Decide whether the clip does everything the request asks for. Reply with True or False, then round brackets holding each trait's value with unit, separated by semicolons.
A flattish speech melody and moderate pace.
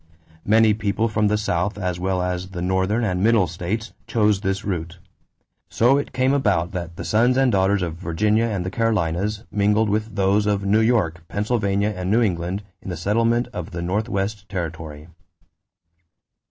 False (3.2 semitones; 170 wpm)